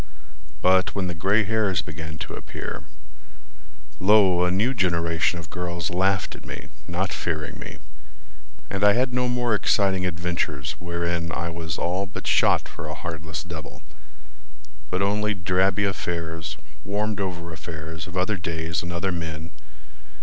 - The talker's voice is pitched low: Yes, very low, 90 Hz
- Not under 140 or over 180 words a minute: Yes, average, 150 wpm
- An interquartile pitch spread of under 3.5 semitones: Yes, average, 2.9 semitones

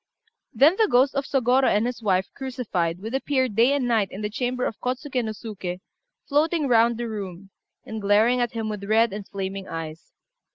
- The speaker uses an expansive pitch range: No, average, 4.2 semitones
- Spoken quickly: No, average, 195 wpm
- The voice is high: Yes, high, 230 Hz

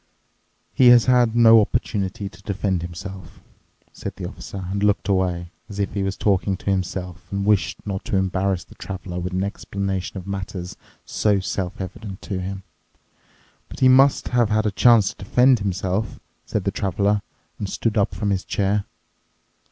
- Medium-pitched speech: No, low, 100 Hz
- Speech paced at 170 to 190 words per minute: Yes, average, 175 wpm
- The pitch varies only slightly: Yes, narrow, 1.9 semitones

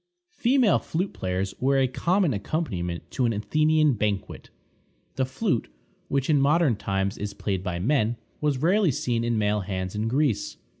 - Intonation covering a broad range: Yes, wide, 7.1 semitones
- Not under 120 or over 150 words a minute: No, average, 160 wpm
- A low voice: Yes, low, 120 Hz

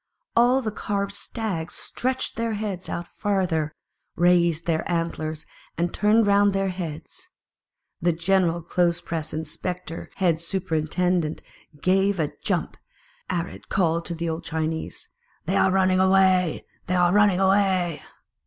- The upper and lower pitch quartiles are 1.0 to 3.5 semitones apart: Yes, average, 2.8 semitones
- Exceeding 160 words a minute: No, average, 155 wpm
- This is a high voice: No, medium, 180 Hz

